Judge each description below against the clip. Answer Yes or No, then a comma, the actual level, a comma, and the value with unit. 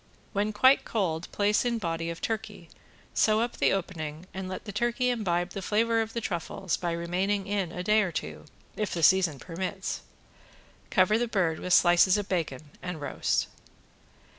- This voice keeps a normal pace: Yes, average, 175 wpm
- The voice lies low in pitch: No, high, 190 Hz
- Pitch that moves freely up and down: No, average, 3.8 semitones